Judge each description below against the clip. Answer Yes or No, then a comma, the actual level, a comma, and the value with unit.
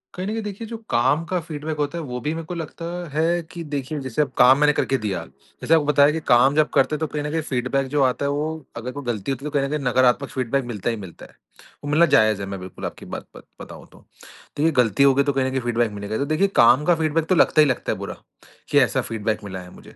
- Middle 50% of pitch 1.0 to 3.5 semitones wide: No, average, 4.2 semitones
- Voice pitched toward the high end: No, medium, 140 Hz